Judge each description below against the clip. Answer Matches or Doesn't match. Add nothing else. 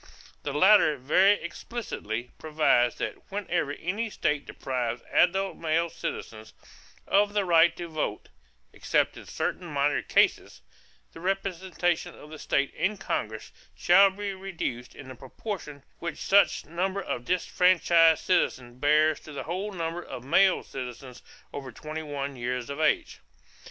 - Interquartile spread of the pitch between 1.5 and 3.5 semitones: Doesn't match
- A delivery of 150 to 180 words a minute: Doesn't match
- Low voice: Doesn't match